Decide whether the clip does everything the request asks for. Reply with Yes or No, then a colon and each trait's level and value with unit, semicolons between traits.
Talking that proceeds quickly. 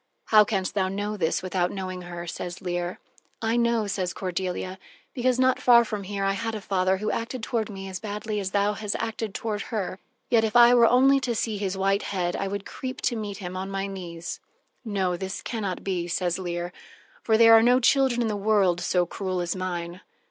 Yes: fast, 215 wpm